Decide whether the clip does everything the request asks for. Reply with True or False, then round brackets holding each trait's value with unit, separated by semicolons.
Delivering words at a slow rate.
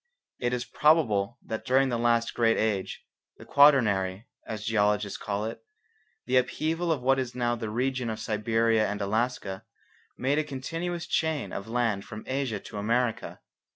False (160 wpm)